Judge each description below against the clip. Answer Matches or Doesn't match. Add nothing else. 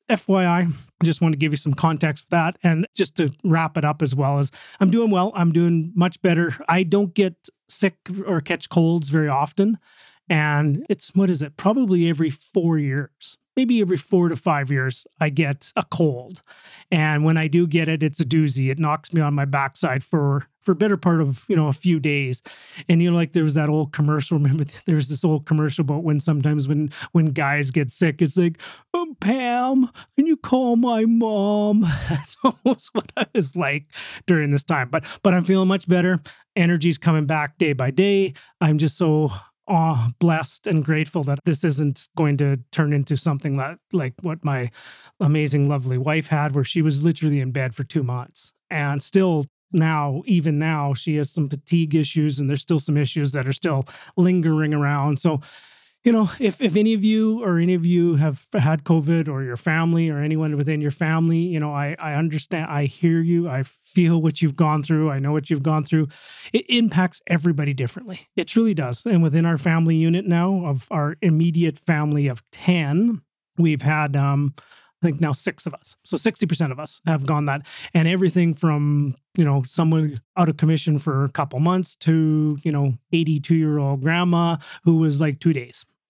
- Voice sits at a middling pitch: Matches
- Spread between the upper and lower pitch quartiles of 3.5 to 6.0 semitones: Doesn't match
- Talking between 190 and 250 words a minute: Matches